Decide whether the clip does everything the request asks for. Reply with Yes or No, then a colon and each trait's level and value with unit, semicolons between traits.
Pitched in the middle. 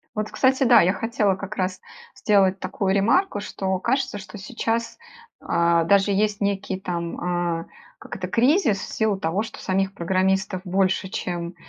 No: high, 195 Hz